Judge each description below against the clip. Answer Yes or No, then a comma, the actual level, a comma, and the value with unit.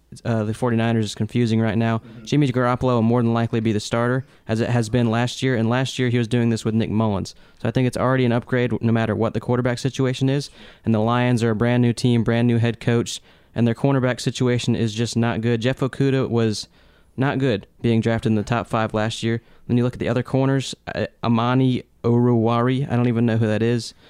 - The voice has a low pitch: Yes, low, 120 Hz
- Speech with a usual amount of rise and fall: No, narrow, 1.7 semitones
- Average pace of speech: No, fast, 240 wpm